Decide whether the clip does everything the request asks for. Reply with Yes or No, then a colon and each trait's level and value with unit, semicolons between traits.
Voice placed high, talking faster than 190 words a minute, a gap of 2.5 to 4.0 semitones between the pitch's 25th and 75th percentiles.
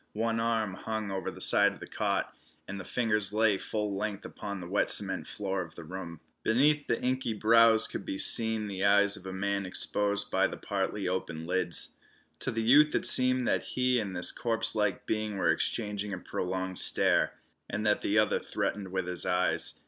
No: low, 105 Hz; average, 200 wpm; average, 2.9 semitones